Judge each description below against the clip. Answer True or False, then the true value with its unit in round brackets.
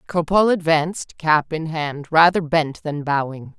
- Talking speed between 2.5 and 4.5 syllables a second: True (4.4 syllables/s)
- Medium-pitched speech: True (160 Hz)